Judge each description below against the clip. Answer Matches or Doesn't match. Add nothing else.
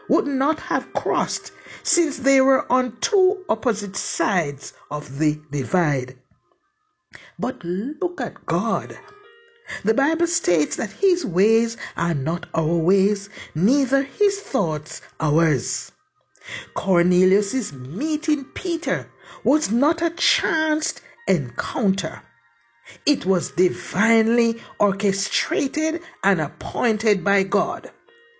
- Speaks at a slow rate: Matches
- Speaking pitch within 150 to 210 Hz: Doesn't match